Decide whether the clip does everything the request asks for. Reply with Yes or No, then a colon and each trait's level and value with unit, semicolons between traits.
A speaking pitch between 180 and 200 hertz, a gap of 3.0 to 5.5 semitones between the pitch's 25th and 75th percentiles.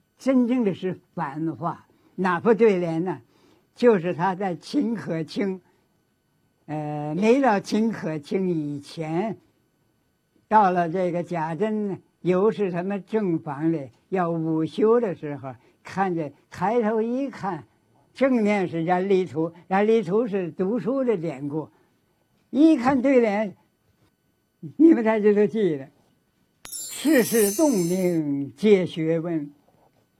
Yes: medium, 185 Hz; average, 5.1 semitones